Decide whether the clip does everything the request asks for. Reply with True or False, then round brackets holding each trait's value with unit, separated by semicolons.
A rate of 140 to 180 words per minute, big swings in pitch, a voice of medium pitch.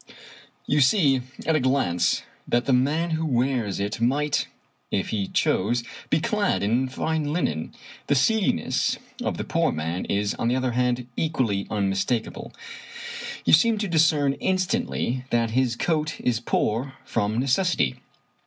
False (145 wpm; 5.7 semitones; 130 Hz)